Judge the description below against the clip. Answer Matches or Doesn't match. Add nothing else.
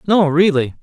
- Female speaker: Doesn't match